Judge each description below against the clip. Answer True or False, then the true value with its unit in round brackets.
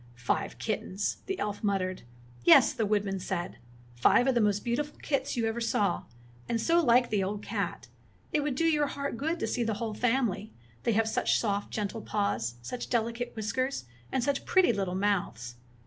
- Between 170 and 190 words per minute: True (185 wpm)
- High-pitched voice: True (225 Hz)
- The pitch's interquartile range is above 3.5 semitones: True (4.1 semitones)